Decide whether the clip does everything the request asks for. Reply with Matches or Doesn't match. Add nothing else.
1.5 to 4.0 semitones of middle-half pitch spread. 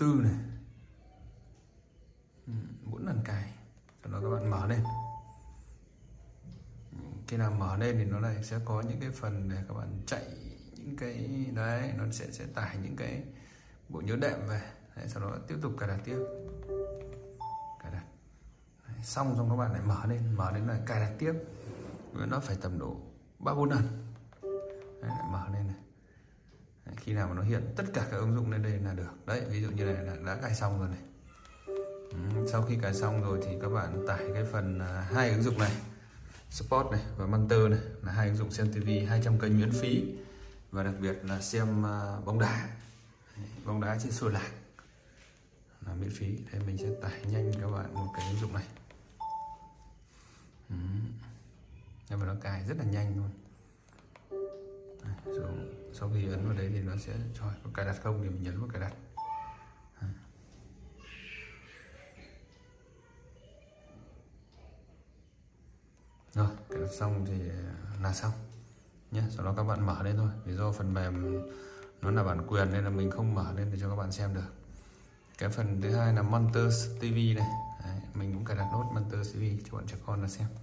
Matches